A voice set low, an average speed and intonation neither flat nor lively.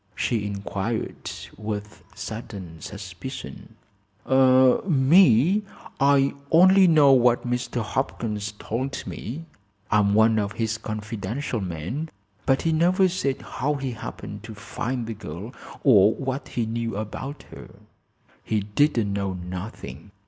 No: low, 115 Hz; slow, 120 wpm; average, 4.7 semitones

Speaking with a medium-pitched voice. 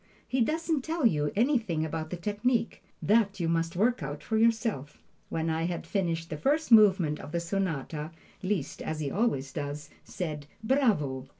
Yes: medium, 175 Hz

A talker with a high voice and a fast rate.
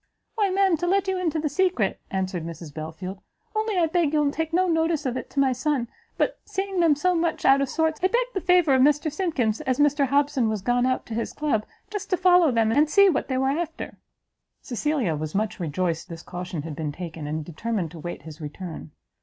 Yes: very high, 275 Hz; fast, 225 wpm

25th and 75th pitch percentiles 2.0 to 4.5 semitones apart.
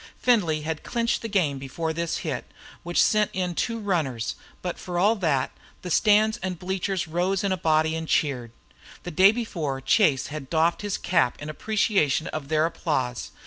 Yes: average, 4.2 semitones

